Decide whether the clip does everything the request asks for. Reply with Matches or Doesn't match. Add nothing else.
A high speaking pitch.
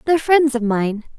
Matches